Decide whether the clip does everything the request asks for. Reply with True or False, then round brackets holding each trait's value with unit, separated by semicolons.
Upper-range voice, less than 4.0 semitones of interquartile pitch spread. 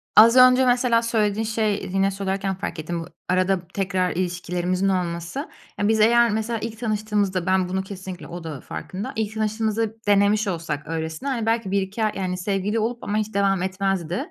True (200 Hz; 3.1 semitones)